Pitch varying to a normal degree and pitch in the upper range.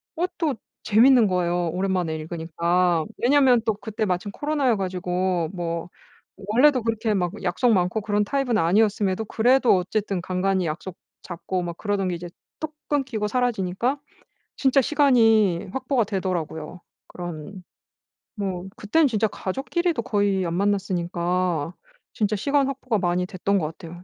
Yes: average, 5.0 semitones; high, 195 Hz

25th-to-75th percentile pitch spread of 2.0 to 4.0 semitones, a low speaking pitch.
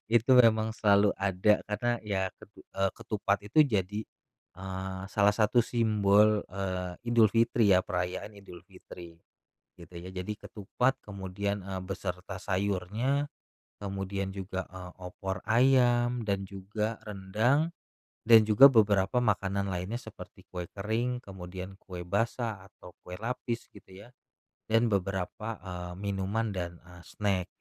Yes: average, 2.9 semitones; low, 100 Hz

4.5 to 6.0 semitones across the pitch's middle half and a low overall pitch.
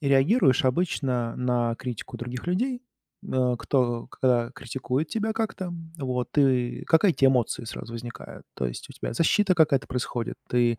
Yes: average, 4.8 semitones; low, 130 Hz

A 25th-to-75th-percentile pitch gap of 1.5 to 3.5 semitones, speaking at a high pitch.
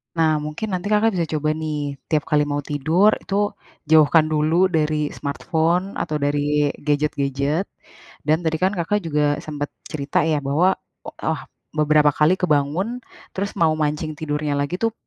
No: narrow, 2.5 semitones; medium, 155 Hz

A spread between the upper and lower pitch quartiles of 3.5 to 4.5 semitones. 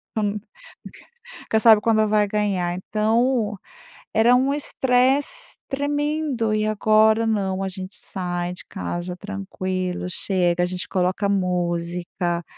Yes: average, 3.8 semitones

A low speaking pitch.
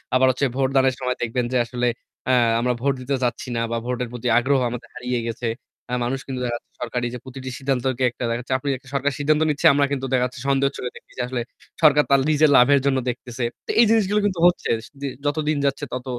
Yes: low, 130 Hz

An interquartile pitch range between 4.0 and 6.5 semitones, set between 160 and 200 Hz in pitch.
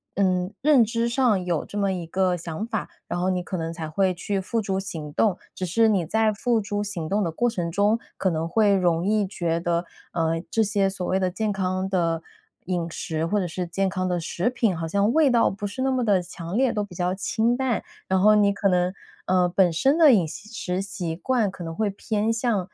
No: average, 3.5 semitones; high, 190 Hz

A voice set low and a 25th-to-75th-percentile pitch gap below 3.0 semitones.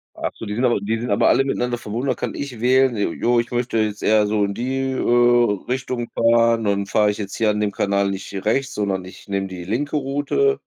No: low, 115 Hz; average, 3.5 semitones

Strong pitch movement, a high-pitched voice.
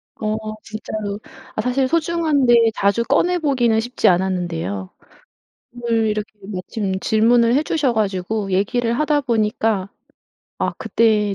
No: average, 3.5 semitones; high, 225 Hz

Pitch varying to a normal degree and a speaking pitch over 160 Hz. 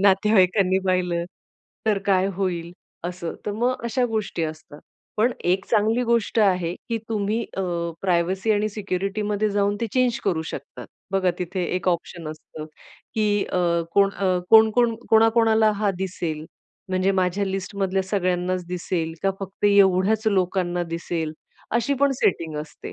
Yes: average, 3.1 semitones; high, 190 Hz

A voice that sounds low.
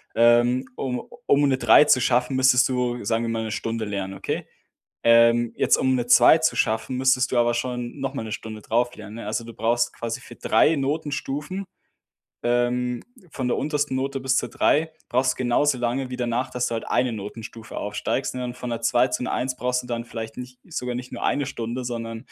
Yes: low, 125 Hz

